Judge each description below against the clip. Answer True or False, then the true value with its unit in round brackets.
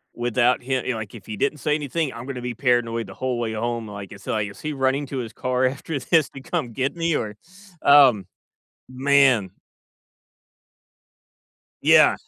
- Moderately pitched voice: False (125 Hz)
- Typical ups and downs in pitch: True (3.2 semitones)